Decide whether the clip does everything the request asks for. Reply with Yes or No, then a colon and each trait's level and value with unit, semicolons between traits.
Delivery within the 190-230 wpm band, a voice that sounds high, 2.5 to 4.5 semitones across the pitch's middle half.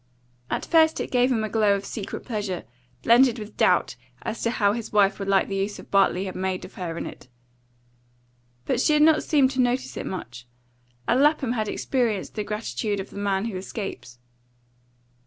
Yes: average, 195 wpm; high, 210 Hz; average, 4.0 semitones